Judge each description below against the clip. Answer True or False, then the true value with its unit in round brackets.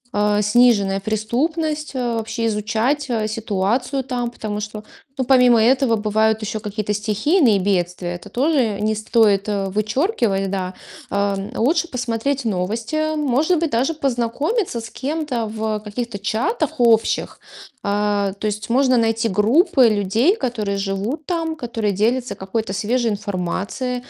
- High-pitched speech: True (225 Hz)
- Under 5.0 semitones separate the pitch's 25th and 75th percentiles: True (3.8 semitones)